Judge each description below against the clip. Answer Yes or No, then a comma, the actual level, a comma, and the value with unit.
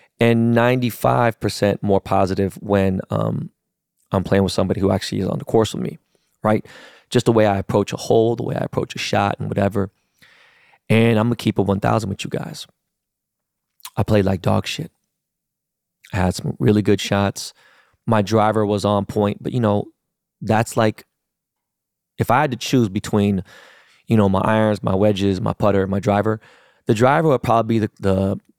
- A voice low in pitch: Yes, low, 105 Hz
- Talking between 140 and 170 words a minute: No, average, 185 wpm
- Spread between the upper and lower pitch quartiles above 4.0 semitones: No, narrow, 2.4 semitones